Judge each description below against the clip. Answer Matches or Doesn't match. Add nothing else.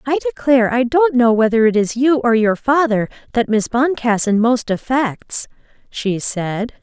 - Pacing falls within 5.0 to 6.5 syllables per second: Doesn't match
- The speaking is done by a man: Doesn't match